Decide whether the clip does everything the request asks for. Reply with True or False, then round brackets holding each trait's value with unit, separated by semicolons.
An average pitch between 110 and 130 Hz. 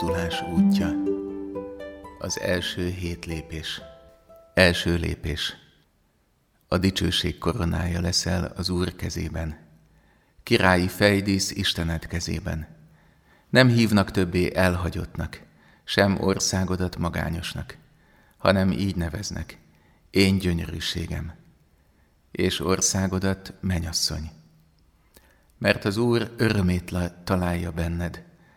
False (90 Hz)